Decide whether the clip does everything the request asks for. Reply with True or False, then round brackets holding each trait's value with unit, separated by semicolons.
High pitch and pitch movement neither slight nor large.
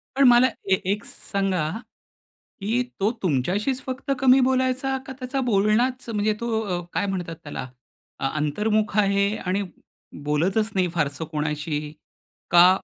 False (200 Hz; 6.3 semitones)